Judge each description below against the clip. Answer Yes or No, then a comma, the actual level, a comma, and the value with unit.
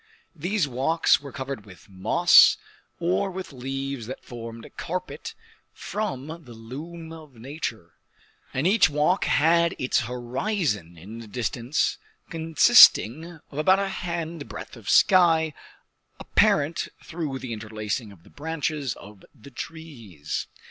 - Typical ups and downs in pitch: No, wide, 6.0 semitones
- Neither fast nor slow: No, slow, 130 wpm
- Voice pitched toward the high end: No, medium, 140 Hz